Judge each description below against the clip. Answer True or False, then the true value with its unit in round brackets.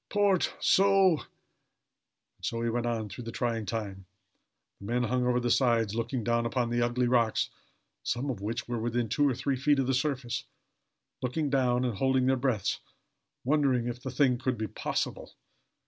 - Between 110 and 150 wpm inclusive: False (180 wpm)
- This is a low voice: True (125 Hz)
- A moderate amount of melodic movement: False (2.2 semitones)